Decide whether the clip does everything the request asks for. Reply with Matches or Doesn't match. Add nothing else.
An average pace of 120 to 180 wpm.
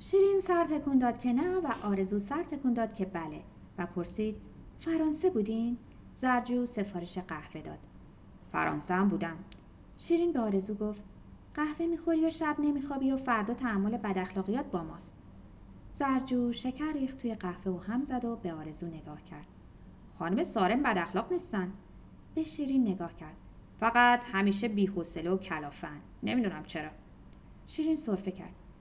Matches